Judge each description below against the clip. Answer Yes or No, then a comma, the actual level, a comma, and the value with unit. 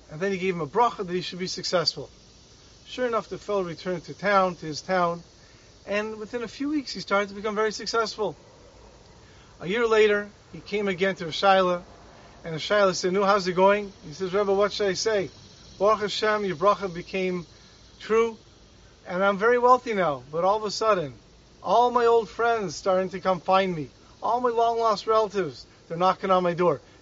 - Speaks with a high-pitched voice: Yes, high, 195 Hz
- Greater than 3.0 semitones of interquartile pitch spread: Yes, average, 3.4 semitones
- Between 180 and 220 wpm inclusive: Yes, average, 200 wpm